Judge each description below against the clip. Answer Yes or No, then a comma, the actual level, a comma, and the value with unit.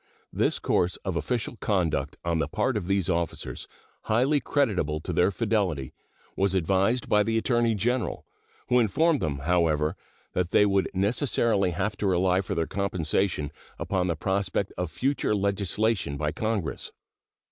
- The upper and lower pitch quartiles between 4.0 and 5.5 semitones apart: Yes, average, 4.5 semitones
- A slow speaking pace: No, average, 150 wpm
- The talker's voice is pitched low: Yes, very low, 95 Hz